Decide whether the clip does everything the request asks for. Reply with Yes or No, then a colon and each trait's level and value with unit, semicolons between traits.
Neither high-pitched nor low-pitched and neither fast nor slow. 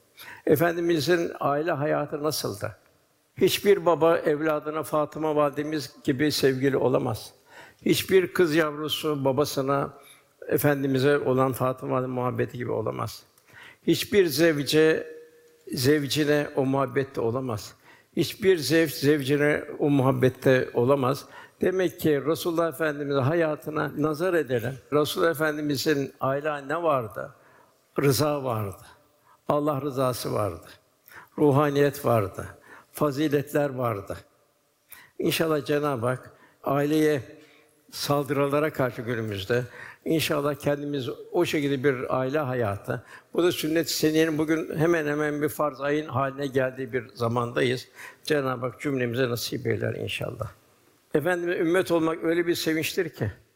Yes: medium, 145 Hz; average, 110 wpm